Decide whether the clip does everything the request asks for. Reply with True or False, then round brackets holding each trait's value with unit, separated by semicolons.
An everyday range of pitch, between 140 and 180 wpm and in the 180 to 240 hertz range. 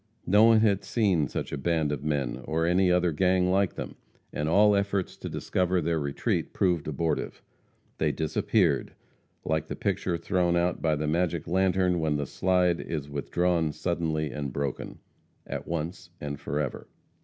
False (3.3 semitones; 165 wpm; 85 Hz)